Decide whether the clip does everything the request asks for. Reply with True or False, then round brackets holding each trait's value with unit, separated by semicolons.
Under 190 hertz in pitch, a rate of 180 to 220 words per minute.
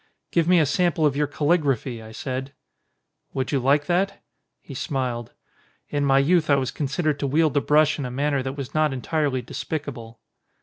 True (140 Hz; 185 wpm)